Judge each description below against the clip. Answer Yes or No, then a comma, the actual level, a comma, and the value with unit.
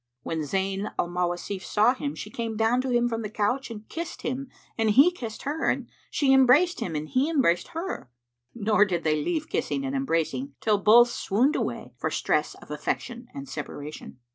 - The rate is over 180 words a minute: Yes, average, 190 wpm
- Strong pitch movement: Yes, wide, 5.9 semitones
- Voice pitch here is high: Yes, high, 230 Hz